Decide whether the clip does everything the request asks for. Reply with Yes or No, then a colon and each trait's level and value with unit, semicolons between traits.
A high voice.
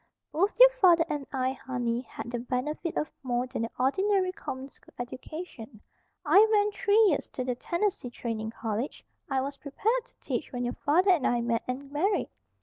Yes: very high, 275 Hz